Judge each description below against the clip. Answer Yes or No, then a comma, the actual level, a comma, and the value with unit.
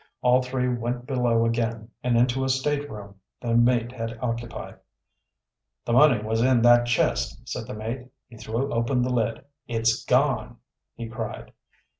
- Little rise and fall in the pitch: Yes, narrow, 1.7 semitones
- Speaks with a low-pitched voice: Yes, low, 120 Hz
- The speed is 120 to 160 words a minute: Yes, average, 155 wpm